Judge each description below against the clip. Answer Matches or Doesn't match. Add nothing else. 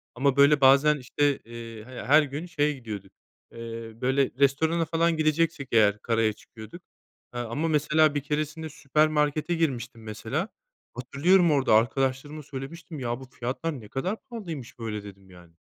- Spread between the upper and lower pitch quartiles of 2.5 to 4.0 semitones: Doesn't match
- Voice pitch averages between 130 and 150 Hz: Matches